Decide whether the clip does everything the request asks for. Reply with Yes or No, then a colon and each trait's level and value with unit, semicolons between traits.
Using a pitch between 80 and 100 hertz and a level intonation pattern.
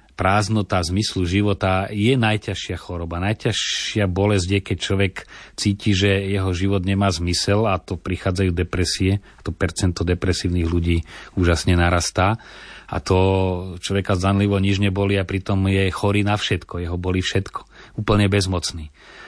Yes: very low, 95 Hz; narrow, 1.8 semitones